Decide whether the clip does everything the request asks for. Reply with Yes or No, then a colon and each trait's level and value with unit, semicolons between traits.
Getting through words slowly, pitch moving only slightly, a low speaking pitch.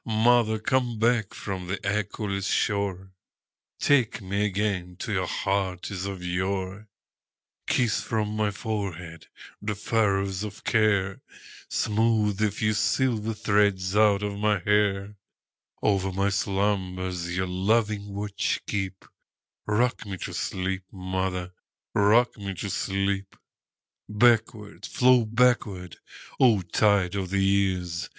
Yes: slow, 105 wpm; narrow, 2.3 semitones; low, 100 Hz